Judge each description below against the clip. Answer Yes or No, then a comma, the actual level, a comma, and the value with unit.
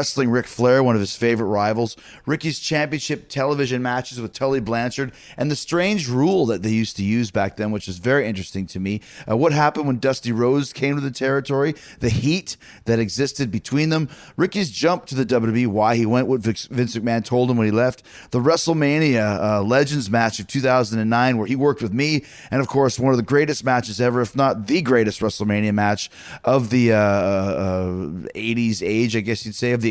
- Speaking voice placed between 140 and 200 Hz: No, low, 125 Hz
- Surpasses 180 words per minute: Yes, fast, 205 wpm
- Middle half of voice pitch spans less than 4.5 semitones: Yes, average, 3.8 semitones